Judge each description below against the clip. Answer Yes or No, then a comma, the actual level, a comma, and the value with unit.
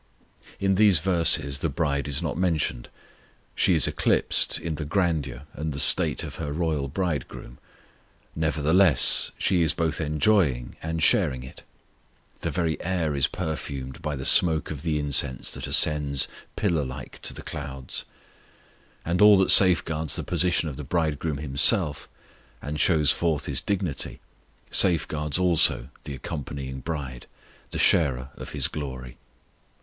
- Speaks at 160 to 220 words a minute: No, average, 145 wpm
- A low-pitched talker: Yes, very low, 75 Hz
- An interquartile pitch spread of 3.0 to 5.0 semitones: Yes, average, 3.3 semitones